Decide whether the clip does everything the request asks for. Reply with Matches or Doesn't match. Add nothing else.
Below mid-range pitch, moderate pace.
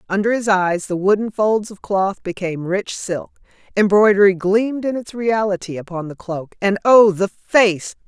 Doesn't match